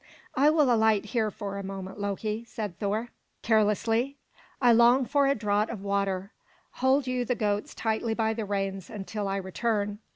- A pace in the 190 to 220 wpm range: No, average, 170 wpm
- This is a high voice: Yes, high, 215 Hz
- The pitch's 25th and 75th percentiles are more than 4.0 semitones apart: No, average, 2.9 semitones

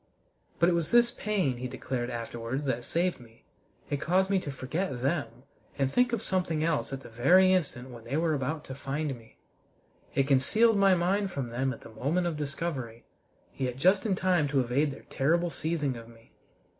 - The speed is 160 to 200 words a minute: Yes, average, 195 wpm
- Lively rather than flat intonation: Yes, wide, 5.8 semitones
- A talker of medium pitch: Yes, medium, 145 Hz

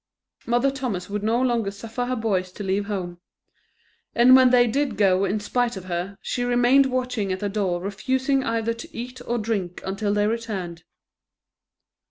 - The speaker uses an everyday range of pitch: Yes, average, 4.0 semitones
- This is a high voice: Yes, high, 220 Hz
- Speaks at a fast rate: No, average, 175 wpm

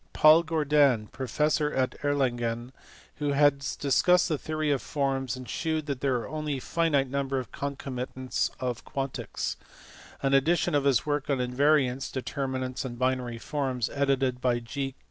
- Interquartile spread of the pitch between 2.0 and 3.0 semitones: Yes, narrow, 2.4 semitones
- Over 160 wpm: No, average, 155 wpm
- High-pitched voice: No, low, 135 Hz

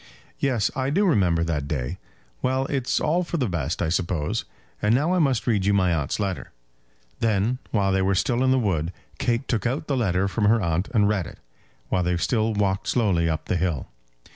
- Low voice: Yes, low, 100 Hz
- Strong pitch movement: Yes, wide, 6.1 semitones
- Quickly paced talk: Yes, fast, 210 wpm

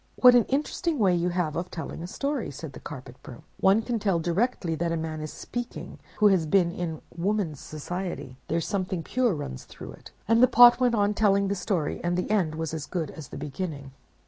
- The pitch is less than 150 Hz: No, medium, 180 Hz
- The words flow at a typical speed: No, fast, 220 wpm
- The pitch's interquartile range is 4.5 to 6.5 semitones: Yes, average, 5.0 semitones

